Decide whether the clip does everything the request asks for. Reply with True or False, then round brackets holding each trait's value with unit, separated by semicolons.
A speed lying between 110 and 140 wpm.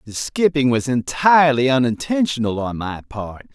True (135 wpm)